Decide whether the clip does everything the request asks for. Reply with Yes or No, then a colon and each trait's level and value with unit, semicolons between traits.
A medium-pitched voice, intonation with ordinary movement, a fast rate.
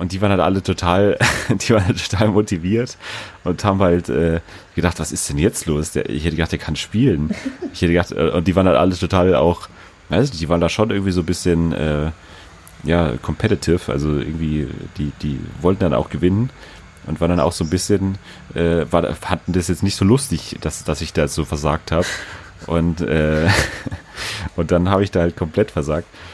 No: very low, 90 Hz; average, 3.0 semitones; fast, 200 wpm